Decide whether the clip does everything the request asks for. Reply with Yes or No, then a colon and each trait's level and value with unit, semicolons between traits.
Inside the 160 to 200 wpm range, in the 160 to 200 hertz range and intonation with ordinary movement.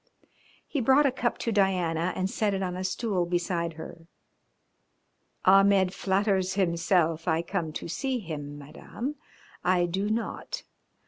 No: average, 140 wpm; medium, 185 Hz; average, 3.1 semitones